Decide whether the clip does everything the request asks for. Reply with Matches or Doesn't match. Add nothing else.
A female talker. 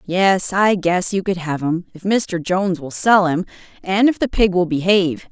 Matches